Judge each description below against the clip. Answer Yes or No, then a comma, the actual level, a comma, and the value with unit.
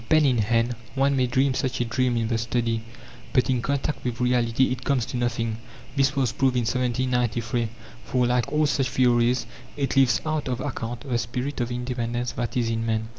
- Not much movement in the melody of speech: Yes, narrow, 1.9 semitones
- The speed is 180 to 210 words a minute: Yes, average, 200 wpm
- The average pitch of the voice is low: Yes, low, 125 Hz